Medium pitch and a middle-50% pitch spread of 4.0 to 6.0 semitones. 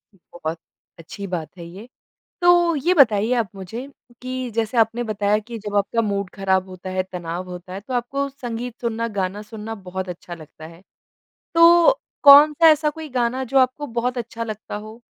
No: high, 225 Hz; wide, 5.4 semitones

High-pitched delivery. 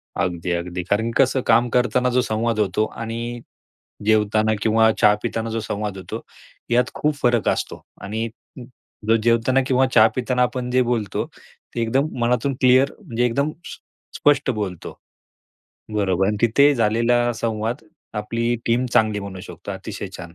No: low, 115 Hz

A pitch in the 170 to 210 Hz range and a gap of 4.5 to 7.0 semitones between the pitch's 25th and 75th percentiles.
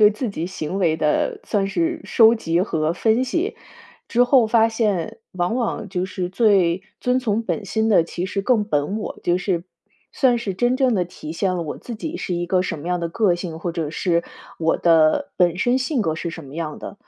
Yes: high, 190 Hz; average, 5.1 semitones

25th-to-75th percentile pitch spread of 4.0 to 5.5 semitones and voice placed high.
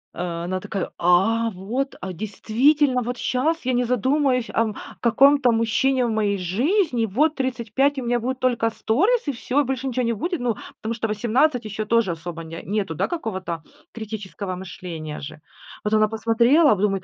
Yes: average, 4.9 semitones; high, 230 Hz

